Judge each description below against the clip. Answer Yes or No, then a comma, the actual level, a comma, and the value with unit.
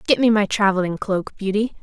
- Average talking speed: Yes, average, 195 wpm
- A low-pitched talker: No, high, 205 Hz